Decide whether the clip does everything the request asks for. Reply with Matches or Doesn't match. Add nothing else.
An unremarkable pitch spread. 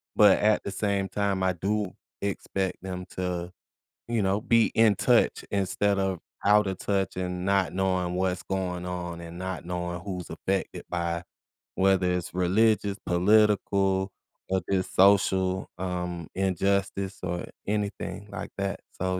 Doesn't match